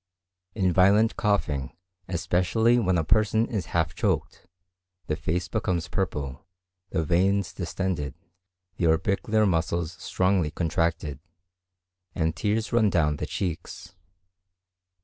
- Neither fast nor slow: No, slow, 110 wpm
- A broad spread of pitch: No, average, 3.6 semitones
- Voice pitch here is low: Yes, very low, 90 Hz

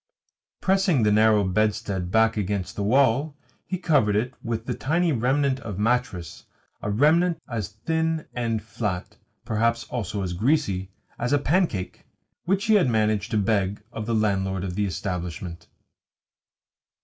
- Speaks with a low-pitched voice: Yes, low, 110 Hz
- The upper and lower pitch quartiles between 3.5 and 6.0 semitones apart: Yes, average, 5.3 semitones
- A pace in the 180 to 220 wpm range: No, average, 150 wpm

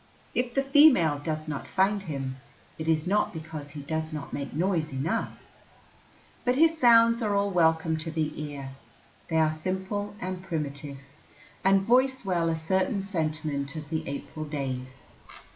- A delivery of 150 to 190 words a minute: Yes, average, 160 wpm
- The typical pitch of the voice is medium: Yes, medium, 160 Hz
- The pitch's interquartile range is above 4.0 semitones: Yes, average, 4.7 semitones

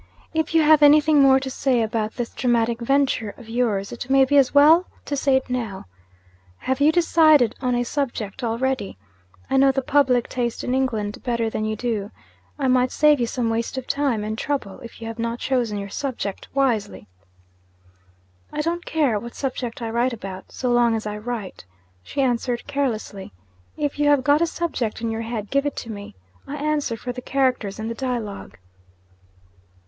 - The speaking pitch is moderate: No, very high, 250 Hz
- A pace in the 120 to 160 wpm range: No, average, 190 wpm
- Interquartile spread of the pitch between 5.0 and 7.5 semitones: No, average, 3.6 semitones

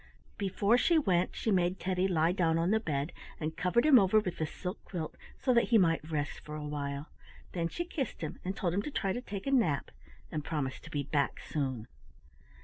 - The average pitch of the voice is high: No, medium, 175 Hz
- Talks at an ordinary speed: No, fast, 220 wpm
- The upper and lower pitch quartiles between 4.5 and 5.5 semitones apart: Yes, average, 5.0 semitones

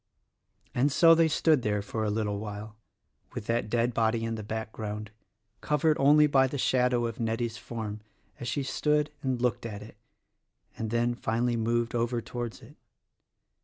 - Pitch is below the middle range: Yes, low, 115 Hz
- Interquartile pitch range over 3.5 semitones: No, narrow, 2.6 semitones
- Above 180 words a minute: No, average, 165 wpm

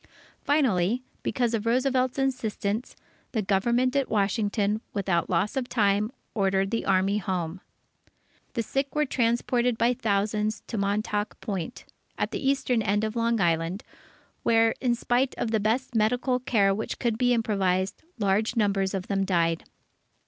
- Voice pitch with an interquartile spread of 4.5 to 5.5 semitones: No, average, 3.6 semitones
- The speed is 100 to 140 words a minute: No, average, 150 wpm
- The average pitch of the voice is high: Yes, high, 215 Hz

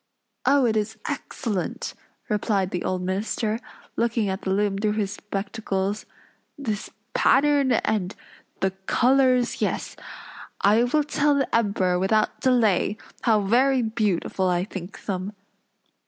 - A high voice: Yes, high, 215 Hz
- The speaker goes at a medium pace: No, slow, 125 wpm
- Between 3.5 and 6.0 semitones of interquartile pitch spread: Yes, average, 3.9 semitones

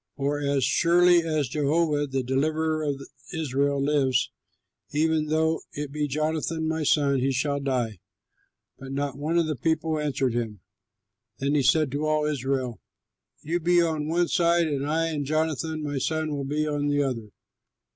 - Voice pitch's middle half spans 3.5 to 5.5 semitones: No, narrow, 2.5 semitones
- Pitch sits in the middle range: Yes, medium, 150 Hz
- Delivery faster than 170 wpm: No, average, 165 wpm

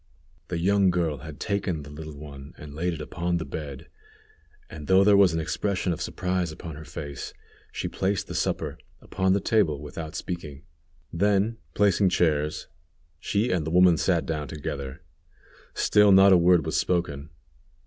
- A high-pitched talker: No, very low, 85 Hz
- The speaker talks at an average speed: Yes, average, 170 wpm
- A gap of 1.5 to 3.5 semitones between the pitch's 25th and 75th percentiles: No, average, 3.9 semitones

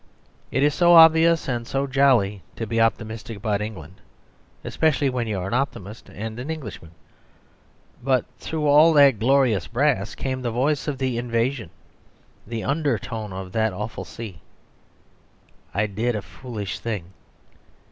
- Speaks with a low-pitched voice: Yes, low, 120 Hz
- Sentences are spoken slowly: No, average, 145 wpm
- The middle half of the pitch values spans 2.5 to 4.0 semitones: No, average, 4.6 semitones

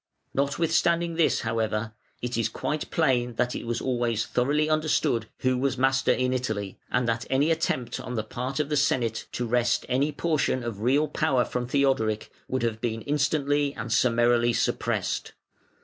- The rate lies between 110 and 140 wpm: No, average, 165 wpm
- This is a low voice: Yes, low, 125 Hz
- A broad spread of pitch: No, average, 3.6 semitones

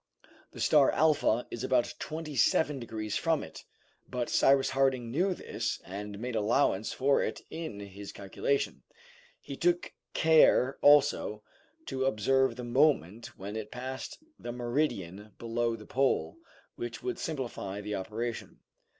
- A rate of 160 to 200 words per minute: No, average, 140 wpm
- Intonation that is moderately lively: Yes, average, 4.7 semitones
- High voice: No, low, 125 Hz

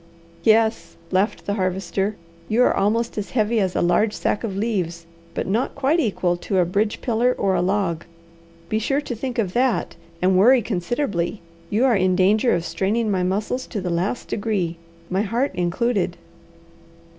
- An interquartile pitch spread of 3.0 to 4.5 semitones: Yes, average, 3.9 semitones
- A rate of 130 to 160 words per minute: No, average, 175 wpm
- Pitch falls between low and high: No, high, 205 Hz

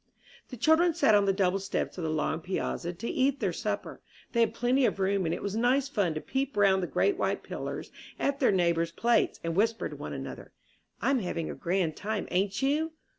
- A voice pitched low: No, high, 205 Hz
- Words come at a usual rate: No, fast, 220 wpm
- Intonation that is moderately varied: No, wide, 6.2 semitones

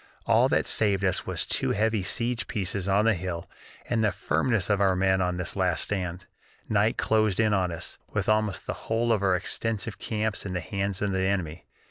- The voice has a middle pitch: No, low, 100 Hz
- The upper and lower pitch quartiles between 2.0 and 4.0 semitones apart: Yes, average, 2.8 semitones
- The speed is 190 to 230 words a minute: Yes, fast, 205 wpm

